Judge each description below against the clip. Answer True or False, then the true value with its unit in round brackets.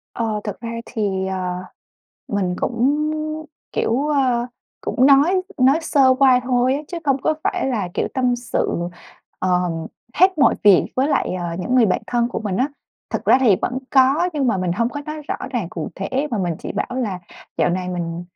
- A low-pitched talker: False (245 Hz)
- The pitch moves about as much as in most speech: False (6.3 semitones)